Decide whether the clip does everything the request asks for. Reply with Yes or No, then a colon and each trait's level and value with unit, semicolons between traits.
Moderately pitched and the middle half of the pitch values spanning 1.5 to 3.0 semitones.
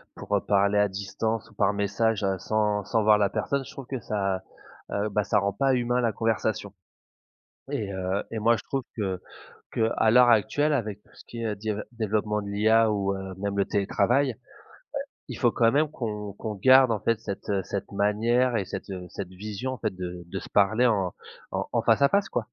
No: low, 105 Hz; narrow, 2.6 semitones